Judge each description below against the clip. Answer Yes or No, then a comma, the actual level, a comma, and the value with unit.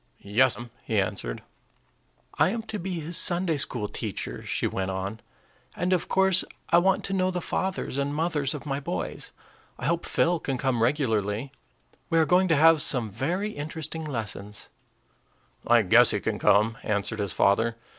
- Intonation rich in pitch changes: Yes, wide, 7.5 semitones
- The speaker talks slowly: No, average, 170 wpm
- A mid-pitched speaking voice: Yes, medium, 145 Hz